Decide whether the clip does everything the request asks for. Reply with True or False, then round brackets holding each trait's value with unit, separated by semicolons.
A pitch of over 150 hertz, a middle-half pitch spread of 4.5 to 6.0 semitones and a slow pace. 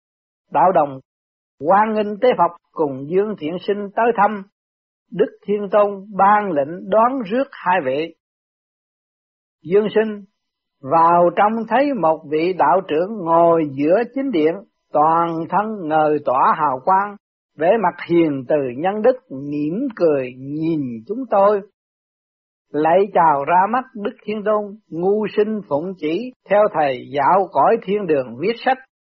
True (190 Hz; 5.3 semitones; 145 wpm)